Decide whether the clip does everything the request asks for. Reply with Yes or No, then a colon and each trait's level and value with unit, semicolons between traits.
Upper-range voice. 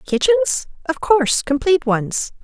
Yes: very high, 270 Hz